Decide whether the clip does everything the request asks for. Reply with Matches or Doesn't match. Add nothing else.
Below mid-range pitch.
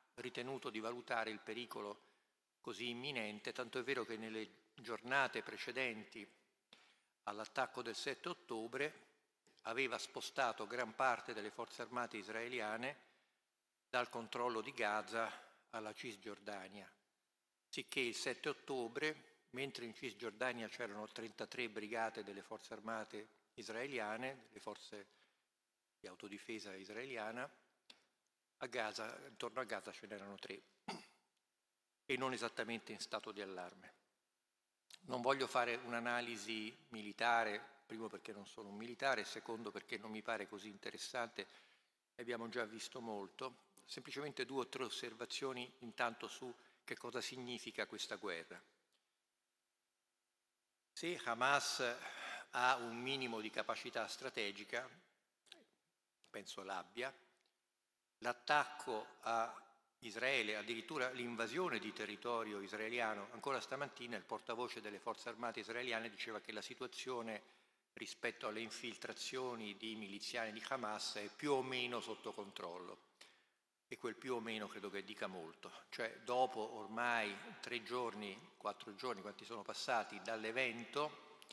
Matches